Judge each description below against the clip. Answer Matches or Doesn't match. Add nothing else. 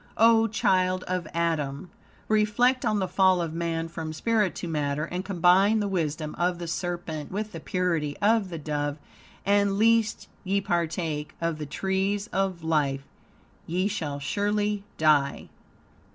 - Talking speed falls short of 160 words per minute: Matches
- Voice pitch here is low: Doesn't match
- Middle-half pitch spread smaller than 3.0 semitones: Doesn't match